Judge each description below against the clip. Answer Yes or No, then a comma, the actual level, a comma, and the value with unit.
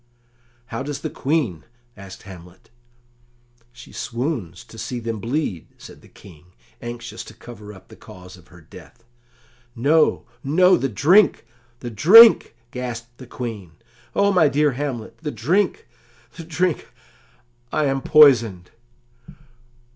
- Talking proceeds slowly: Yes, slow, 130 wpm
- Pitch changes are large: Yes, wide, 6.4 semitones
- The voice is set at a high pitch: No, low, 120 Hz